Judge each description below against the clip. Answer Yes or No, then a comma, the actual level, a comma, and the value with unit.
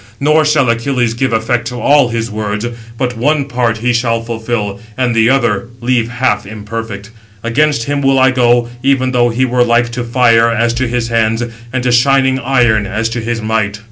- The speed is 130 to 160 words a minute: No, average, 195 wpm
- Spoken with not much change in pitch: Yes, narrow, 2.1 semitones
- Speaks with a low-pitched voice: Yes, low, 120 Hz